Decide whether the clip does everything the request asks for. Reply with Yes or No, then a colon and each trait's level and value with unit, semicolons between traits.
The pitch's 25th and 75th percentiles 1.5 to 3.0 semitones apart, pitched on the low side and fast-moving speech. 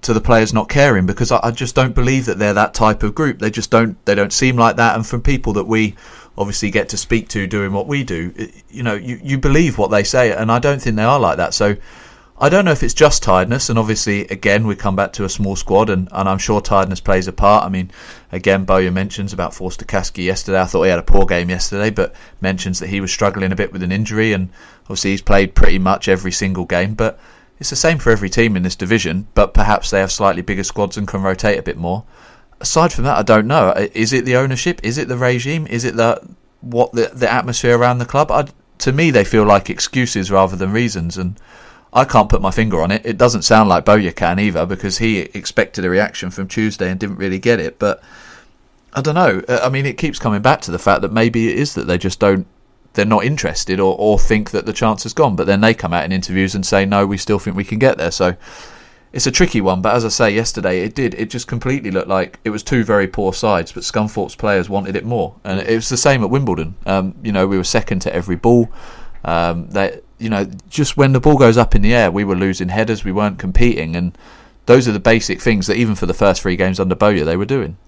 No: average, 3.7 semitones; low, 105 Hz; fast, 255 wpm